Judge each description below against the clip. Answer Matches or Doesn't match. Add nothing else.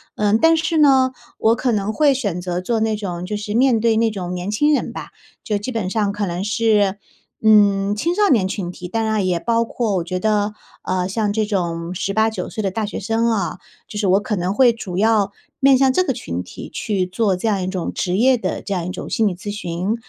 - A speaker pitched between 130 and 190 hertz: Doesn't match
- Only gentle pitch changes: Doesn't match